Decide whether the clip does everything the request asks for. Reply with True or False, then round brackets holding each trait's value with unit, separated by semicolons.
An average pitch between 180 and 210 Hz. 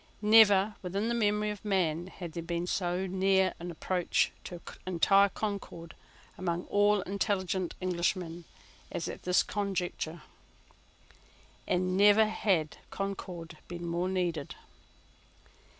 True (185 Hz)